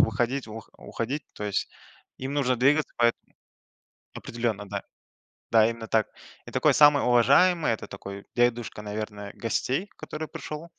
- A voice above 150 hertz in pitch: No, low, 120 Hz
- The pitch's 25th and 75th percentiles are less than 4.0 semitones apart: No, average, 4.6 semitones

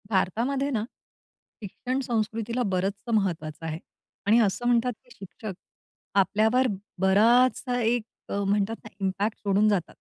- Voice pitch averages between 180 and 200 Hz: No, high, 215 Hz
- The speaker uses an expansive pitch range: No, average, 3.7 semitones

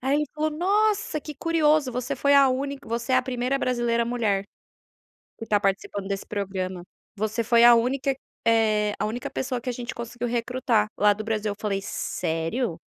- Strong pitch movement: No, average, 4.2 semitones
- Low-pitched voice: No, high, 235 Hz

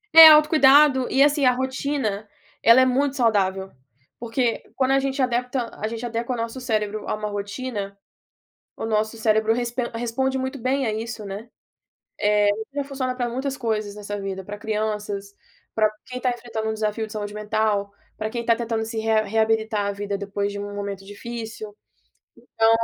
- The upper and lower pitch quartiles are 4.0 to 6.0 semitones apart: No, average, 3.3 semitones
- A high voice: Yes, high, 225 Hz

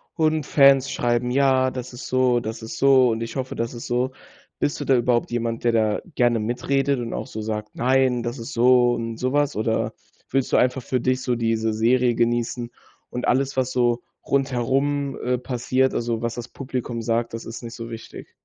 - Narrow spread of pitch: Yes, narrow, 2.0 semitones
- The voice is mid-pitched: No, low, 120 Hz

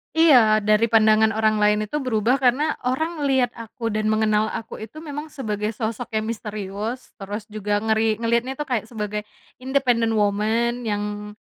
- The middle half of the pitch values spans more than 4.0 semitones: No, average, 2.7 semitones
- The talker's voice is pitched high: Yes, high, 220 Hz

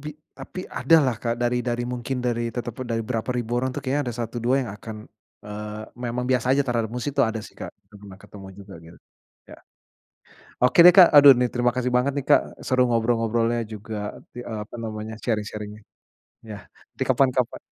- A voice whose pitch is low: Yes, low, 120 Hz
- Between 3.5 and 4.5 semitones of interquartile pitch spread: No, average, 2.7 semitones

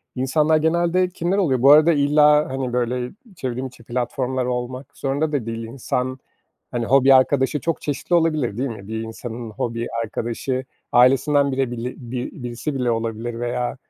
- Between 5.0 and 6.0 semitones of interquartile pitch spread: No, average, 3.2 semitones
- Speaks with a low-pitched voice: Yes, low, 130 Hz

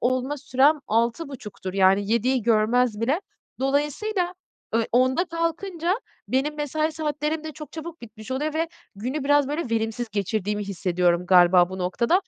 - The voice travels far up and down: Yes, wide, 6.2 semitones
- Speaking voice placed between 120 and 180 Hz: No, very high, 255 Hz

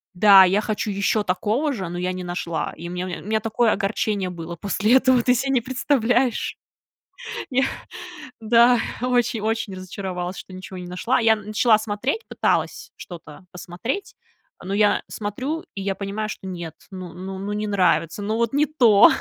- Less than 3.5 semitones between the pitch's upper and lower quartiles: No, average, 4.2 semitones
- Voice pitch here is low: No, high, 205 Hz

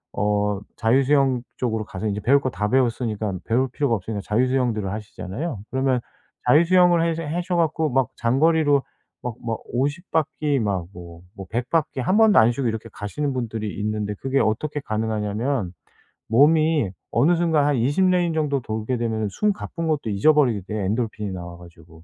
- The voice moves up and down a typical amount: No, wide, 5.7 semitones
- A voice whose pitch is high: No, low, 125 Hz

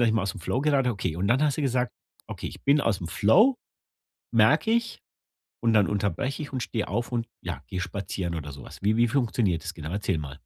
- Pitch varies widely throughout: Yes, wide, 5.9 semitones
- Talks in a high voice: No, low, 110 Hz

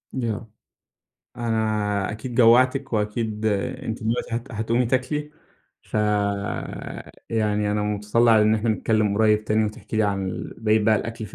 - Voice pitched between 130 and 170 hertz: No, low, 110 Hz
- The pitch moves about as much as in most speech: No, narrow, 1.8 semitones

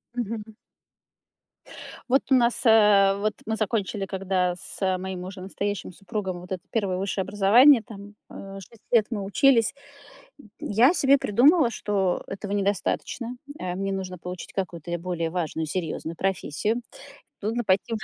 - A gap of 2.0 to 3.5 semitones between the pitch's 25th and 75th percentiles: Yes, average, 3.2 semitones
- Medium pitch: No, high, 195 Hz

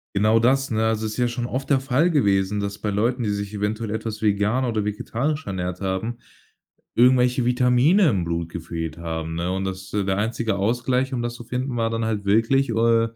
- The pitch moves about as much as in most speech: Yes, average, 3.7 semitones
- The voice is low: Yes, low, 110 Hz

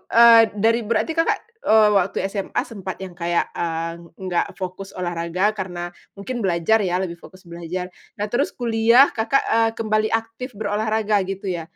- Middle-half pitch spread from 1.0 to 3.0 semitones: No, average, 3.9 semitones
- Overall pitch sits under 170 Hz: No, high, 200 Hz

